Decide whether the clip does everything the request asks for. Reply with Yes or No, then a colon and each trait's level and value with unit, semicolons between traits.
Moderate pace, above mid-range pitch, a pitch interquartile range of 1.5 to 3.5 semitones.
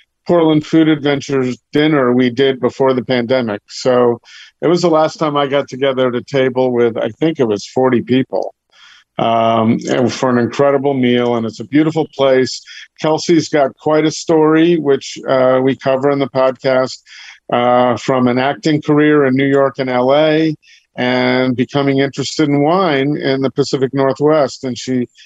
No: average, 170 wpm; low, 135 Hz; average, 2.8 semitones